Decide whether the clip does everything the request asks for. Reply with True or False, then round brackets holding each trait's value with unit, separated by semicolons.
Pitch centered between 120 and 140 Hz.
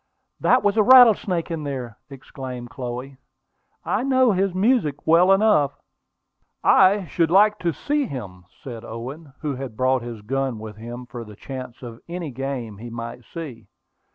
True (135 Hz)